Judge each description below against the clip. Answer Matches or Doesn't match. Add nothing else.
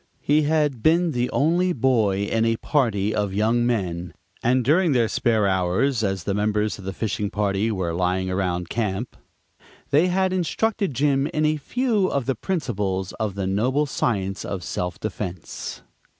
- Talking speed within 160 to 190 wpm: Matches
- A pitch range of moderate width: Doesn't match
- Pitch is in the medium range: Doesn't match